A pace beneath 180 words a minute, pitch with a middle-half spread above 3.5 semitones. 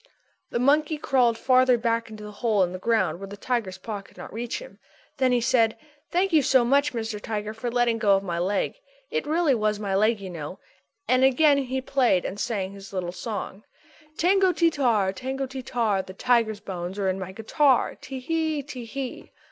No: fast, 205 wpm; average, 4.9 semitones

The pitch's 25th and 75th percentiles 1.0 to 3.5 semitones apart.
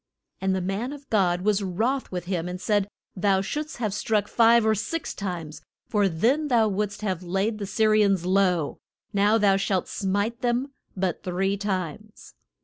Yes: average, 2.8 semitones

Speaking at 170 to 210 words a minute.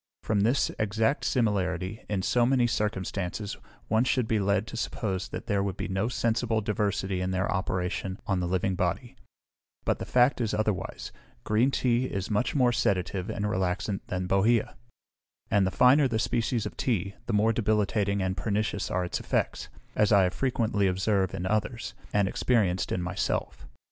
Yes: average, 175 wpm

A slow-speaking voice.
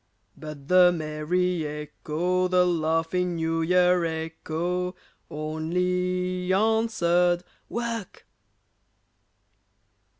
Yes: slow, 70 wpm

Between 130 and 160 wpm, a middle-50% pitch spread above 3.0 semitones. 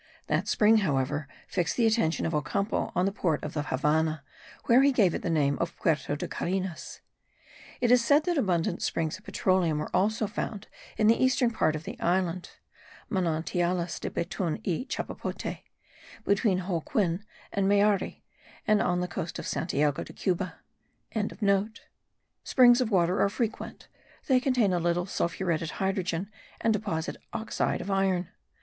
Yes: average, 155 wpm; average, 4.3 semitones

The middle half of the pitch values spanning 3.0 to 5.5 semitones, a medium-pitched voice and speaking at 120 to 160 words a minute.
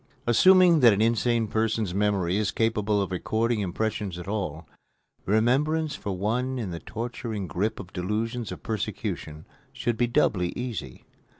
No: average, 3.5 semitones; low, 110 Hz; average, 145 wpm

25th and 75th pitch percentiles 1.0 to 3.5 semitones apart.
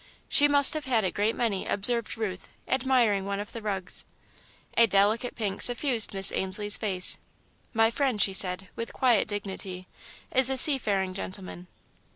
No: average, 4.0 semitones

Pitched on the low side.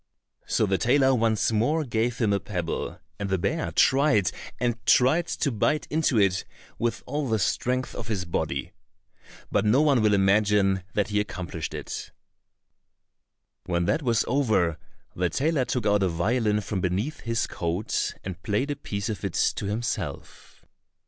Yes: low, 110 Hz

